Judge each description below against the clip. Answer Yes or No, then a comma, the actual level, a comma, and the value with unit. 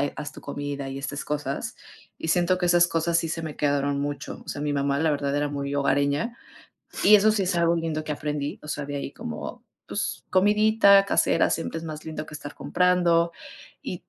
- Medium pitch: Yes, medium, 155 Hz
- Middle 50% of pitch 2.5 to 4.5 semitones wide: Yes, average, 3.5 semitones